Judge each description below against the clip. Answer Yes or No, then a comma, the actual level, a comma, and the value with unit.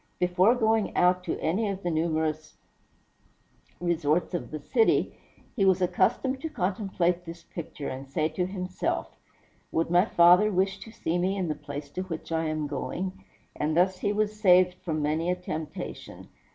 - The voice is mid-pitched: Yes, medium, 180 Hz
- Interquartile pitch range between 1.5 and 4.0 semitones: Yes, average, 3.3 semitones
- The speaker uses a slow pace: No, average, 170 wpm